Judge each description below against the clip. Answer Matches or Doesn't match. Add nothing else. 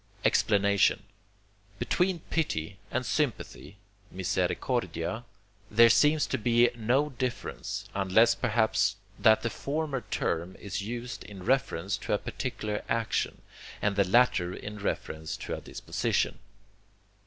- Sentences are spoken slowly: Matches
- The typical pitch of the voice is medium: Doesn't match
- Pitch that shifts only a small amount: Doesn't match